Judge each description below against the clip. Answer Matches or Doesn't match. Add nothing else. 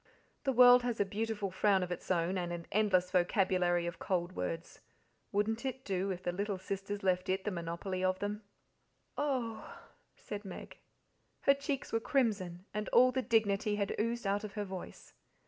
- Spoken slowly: Doesn't match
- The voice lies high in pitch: Matches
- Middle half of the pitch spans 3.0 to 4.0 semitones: Matches